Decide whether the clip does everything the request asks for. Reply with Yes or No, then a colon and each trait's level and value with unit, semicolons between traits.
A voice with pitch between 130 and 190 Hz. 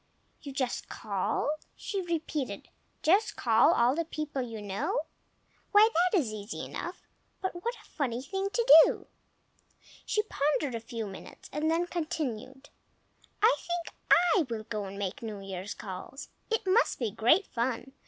No: very high, 280 Hz